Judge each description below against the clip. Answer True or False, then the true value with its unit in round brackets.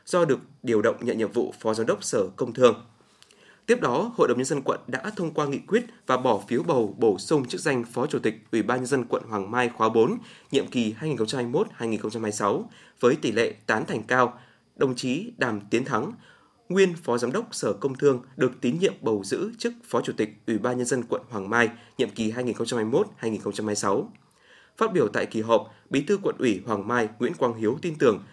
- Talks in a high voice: False (125 Hz)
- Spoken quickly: False (215 wpm)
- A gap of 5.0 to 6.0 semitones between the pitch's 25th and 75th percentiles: False (3.9 semitones)